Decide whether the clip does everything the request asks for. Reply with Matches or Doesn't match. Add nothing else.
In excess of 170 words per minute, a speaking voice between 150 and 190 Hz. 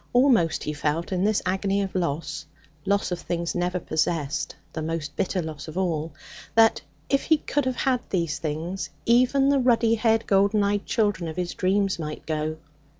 Matches